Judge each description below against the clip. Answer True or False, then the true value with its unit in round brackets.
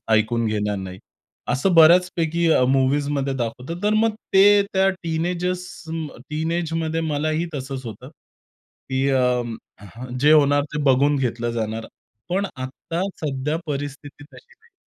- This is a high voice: False (145 Hz)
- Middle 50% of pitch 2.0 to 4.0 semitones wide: False (4.4 semitones)